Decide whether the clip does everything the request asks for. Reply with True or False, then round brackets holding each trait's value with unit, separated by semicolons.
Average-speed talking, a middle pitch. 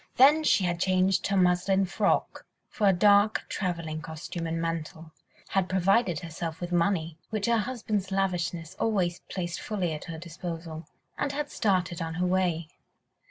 True (150 wpm; 180 Hz)